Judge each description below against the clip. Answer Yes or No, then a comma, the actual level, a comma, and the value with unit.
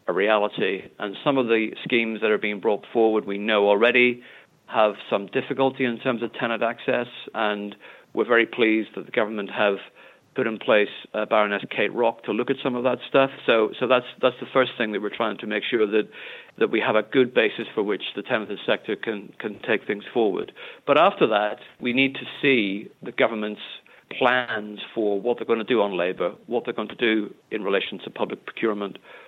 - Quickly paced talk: Yes, fast, 210 wpm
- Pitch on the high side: No, low, 115 Hz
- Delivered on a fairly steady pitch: No, average, 4.0 semitones